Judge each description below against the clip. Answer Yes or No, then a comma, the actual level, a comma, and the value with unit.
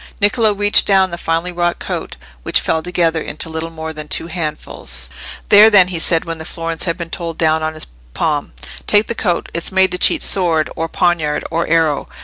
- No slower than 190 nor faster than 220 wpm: Yes, fast, 205 wpm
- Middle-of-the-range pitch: Yes, medium, 165 Hz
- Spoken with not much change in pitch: Yes, narrow, 2.2 semitones